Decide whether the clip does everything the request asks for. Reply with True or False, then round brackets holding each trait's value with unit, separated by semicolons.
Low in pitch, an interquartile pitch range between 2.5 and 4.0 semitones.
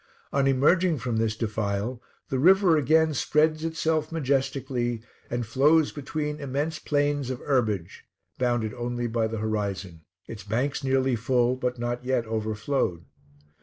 False (125 Hz; 4.4 semitones)